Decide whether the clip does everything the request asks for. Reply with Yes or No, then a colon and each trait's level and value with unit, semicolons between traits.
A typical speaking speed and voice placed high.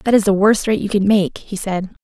No: fast, 295 wpm; high, 200 Hz